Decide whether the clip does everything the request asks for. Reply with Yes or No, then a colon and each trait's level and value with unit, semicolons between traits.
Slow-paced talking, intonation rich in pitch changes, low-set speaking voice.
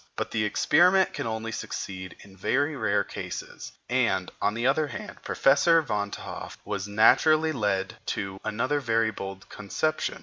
No: average, 155 wpm; wide, 6.2 semitones; low, 110 Hz